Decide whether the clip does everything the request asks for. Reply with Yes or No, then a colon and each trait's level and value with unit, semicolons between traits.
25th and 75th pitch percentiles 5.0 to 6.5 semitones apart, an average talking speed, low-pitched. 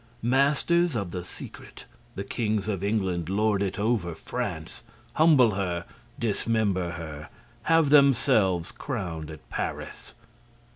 No: average, 5.3 semitones; slow, 115 wpm; low, 100 Hz